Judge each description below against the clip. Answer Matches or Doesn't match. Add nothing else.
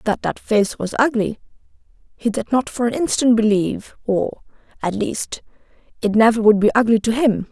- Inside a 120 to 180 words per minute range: Matches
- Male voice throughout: Doesn't match